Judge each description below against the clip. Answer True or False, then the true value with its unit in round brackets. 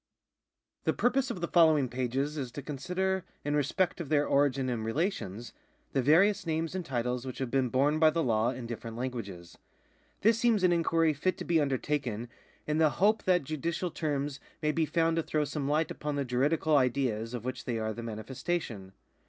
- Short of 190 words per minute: False (195 wpm)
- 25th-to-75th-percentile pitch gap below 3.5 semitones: False (4.8 semitones)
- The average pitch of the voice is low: False (145 Hz)